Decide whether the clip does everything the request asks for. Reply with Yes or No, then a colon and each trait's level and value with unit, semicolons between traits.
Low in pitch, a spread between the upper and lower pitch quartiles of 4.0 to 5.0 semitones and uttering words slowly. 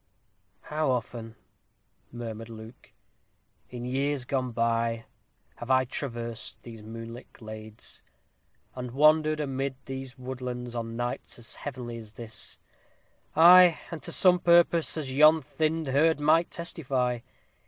Yes: low, 130 Hz; average, 4.6 semitones; slow, 120 wpm